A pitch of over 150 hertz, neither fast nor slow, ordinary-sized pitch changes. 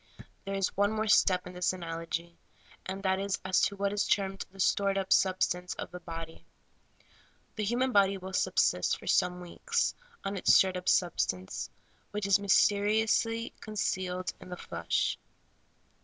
No: high, 190 Hz; average, 165 wpm; narrow, 2.0 semitones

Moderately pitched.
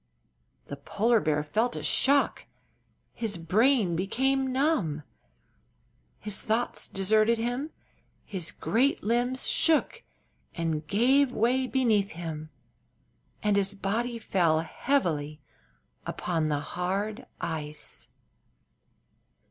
No: high, 210 Hz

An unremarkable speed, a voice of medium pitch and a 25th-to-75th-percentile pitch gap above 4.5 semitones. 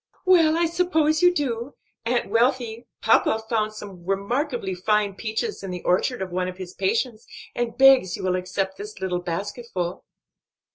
No: average, 160 wpm; high, 215 Hz; average, 5.0 semitones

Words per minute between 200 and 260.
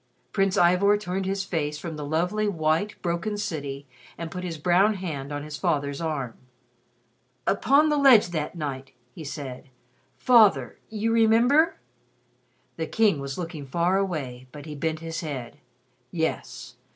No: average, 155 wpm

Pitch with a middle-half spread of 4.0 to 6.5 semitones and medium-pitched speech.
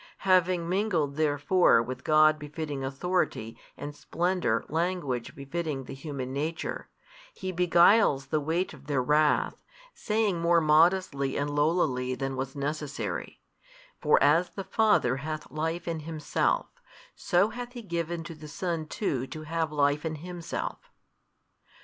No: average, 3.6 semitones; medium, 155 Hz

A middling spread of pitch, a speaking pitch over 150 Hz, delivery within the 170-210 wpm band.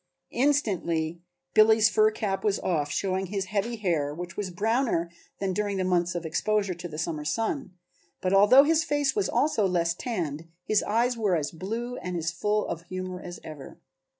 Yes: average, 4.2 semitones; high, 190 Hz; average, 180 wpm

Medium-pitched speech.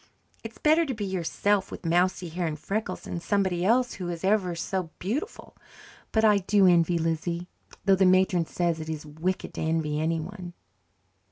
Yes: medium, 180 Hz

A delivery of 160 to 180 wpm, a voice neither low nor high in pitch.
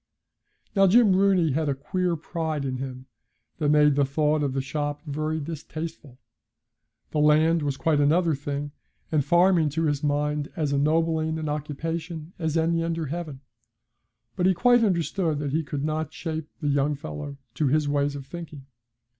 Yes: average, 170 wpm; medium, 155 Hz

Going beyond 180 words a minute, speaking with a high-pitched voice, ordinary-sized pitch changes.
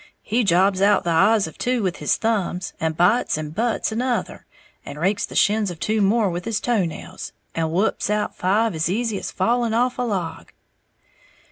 Yes: average, 195 wpm; high, 205 Hz; average, 4.3 semitones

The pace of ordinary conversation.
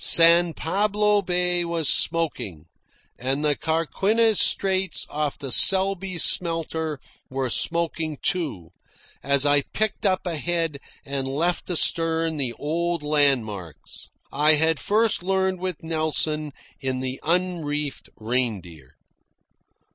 No: slow, 110 wpm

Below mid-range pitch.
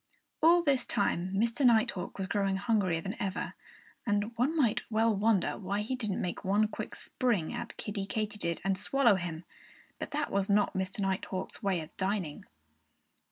No: high, 205 Hz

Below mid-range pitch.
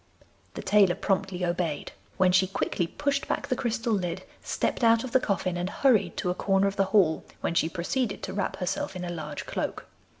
No: high, 190 Hz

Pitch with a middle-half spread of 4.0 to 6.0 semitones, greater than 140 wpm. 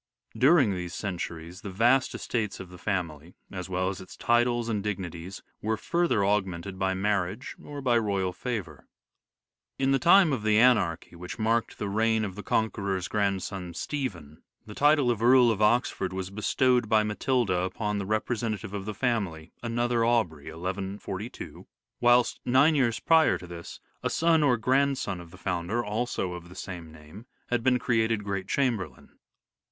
Yes: average, 4.6 semitones; average, 170 wpm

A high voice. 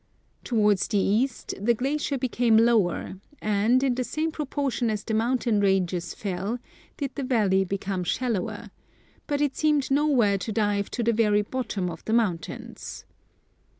Yes: high, 225 Hz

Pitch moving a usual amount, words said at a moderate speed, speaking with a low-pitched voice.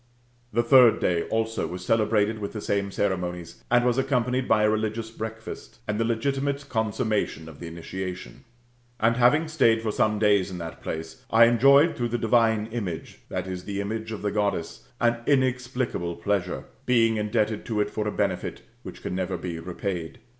Yes: average, 3.9 semitones; average, 175 wpm; low, 110 Hz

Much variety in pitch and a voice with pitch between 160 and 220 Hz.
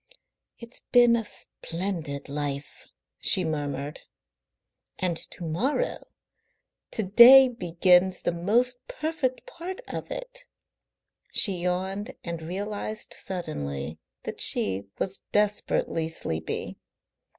Yes: wide, 6.7 semitones; medium, 185 Hz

